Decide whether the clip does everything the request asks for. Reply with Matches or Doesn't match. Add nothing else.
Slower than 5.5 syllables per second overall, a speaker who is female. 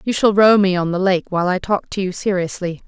Doesn't match